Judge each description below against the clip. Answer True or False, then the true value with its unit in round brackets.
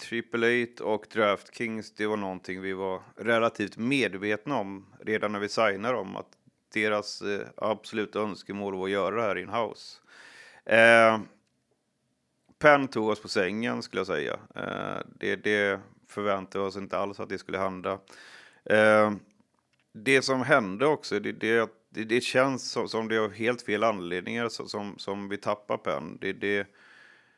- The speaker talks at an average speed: True (165 wpm)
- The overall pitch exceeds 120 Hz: False (105 Hz)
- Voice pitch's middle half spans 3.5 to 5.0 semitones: False (2.4 semitones)